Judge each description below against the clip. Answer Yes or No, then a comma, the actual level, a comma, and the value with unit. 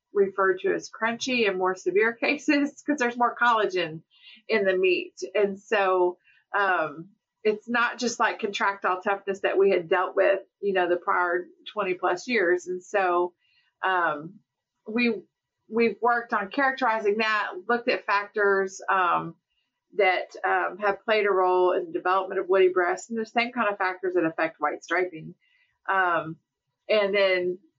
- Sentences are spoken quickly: No, average, 160 wpm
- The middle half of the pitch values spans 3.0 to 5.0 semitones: Yes, average, 4.0 semitones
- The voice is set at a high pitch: Yes, high, 195 Hz